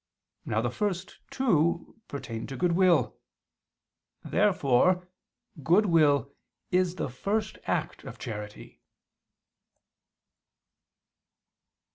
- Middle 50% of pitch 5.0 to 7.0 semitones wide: Yes, wide, 5.5 semitones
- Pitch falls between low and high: Yes, medium, 170 Hz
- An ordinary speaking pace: No, slow, 75 wpm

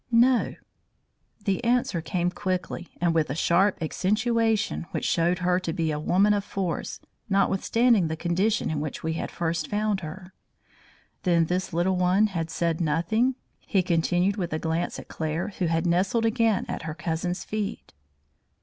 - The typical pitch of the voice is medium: Yes, medium, 180 Hz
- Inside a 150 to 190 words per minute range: Yes, average, 165 wpm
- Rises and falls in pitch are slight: No, average, 3.8 semitones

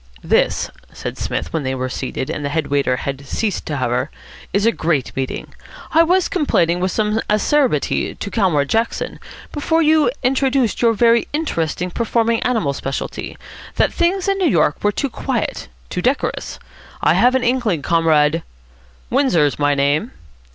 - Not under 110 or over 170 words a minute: Yes, average, 165 wpm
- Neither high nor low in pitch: No, high, 200 Hz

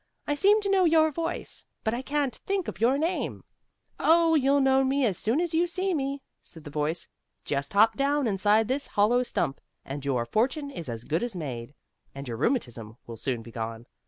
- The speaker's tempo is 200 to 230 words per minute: Yes, fast, 205 wpm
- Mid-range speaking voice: No, high, 240 Hz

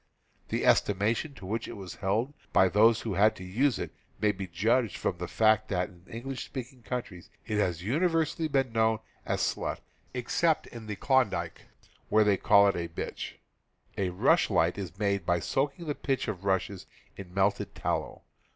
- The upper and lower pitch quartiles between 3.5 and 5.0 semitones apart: Yes, average, 4.5 semitones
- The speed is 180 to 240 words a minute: Yes, average, 185 wpm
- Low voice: Yes, low, 105 Hz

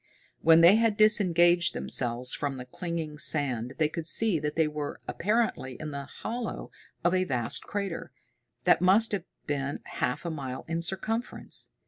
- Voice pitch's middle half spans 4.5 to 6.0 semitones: Yes, average, 5.2 semitones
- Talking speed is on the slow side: No, average, 160 wpm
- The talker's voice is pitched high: No, medium, 165 Hz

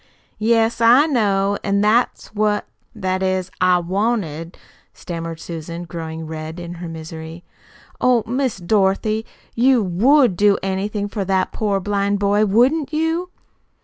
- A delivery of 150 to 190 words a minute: No, average, 140 wpm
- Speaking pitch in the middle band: No, high, 200 Hz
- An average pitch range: Yes, average, 4.4 semitones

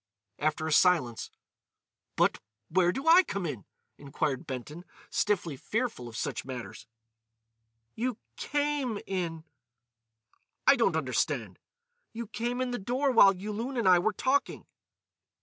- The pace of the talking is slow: Yes, slow, 125 wpm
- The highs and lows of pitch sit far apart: Yes, wide, 8.6 semitones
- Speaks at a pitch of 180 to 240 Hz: Yes, high, 190 Hz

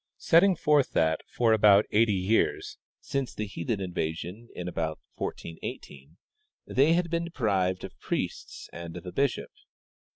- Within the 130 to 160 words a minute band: Yes, average, 150 wpm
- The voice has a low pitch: Yes, low, 105 Hz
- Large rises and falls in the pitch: Yes, wide, 7.8 semitones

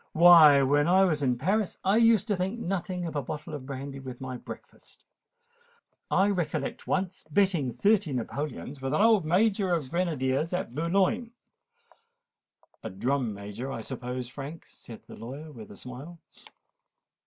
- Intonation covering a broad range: Yes, wide, 6.0 semitones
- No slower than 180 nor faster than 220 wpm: No, average, 155 wpm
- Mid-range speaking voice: Yes, medium, 150 Hz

